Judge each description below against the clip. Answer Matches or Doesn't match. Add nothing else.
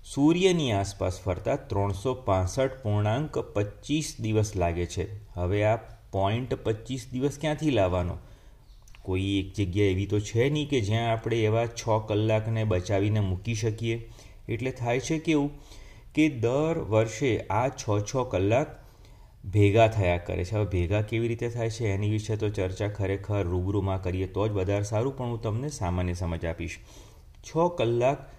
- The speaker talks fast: Matches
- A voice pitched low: Matches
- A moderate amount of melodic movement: Matches